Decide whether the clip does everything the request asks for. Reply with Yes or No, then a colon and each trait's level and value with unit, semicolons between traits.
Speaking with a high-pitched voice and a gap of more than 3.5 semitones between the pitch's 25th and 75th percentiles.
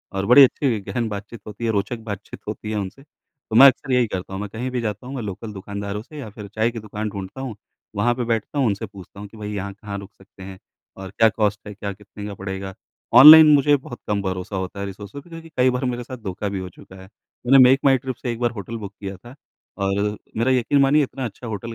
No: low, 105 Hz; average, 3.9 semitones